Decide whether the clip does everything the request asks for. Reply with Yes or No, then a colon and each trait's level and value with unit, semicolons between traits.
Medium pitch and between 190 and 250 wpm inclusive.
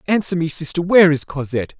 Yes: medium, 160 Hz; average, 200 wpm